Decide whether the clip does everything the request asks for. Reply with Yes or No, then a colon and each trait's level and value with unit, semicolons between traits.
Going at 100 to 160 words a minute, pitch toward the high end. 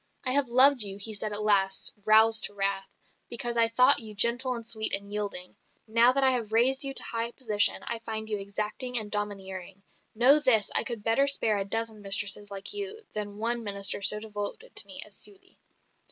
No: fast, 205 wpm; high, 220 Hz